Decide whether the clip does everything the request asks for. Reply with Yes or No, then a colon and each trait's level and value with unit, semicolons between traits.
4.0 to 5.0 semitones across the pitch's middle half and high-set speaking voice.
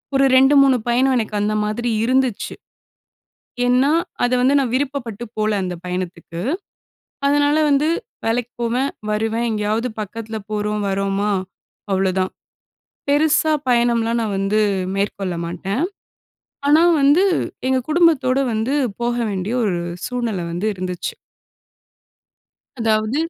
Yes: average, 4.4 semitones; high, 230 Hz